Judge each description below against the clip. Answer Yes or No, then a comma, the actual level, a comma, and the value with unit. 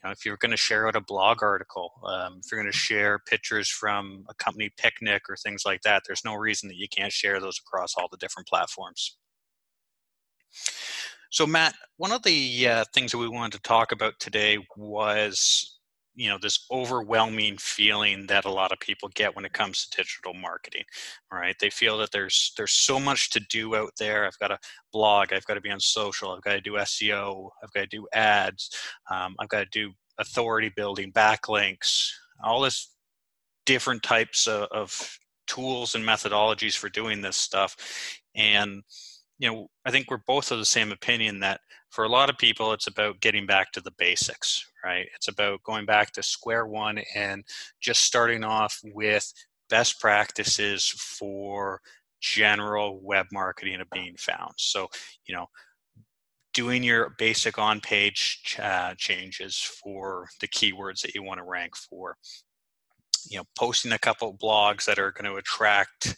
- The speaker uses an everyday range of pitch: No, narrow, 1.7 semitones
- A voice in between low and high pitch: No, low, 105 Hz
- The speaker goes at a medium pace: Yes, average, 180 wpm